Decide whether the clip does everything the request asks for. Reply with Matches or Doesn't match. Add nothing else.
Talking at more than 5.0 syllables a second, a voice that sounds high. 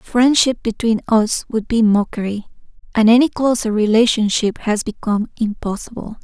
Doesn't match